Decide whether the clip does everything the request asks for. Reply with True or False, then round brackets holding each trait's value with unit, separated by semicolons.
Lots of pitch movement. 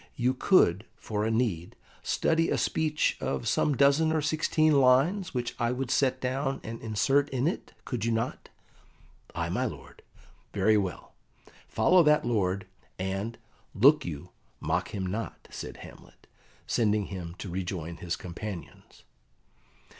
True (6.5 semitones)